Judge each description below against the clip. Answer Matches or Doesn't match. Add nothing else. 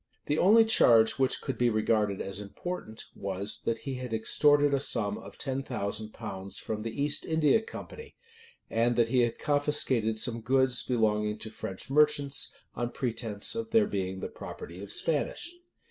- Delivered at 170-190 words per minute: Matches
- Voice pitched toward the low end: Matches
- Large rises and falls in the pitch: Doesn't match